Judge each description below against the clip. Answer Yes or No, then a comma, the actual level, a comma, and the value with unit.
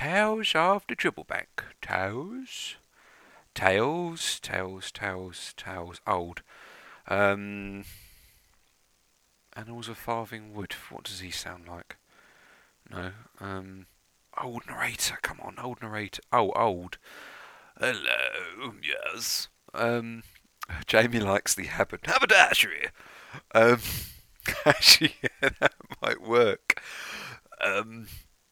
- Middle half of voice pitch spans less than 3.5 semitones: No, average, 3.8 semitones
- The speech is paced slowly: Yes, slow, 95 wpm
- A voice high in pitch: No, low, 100 Hz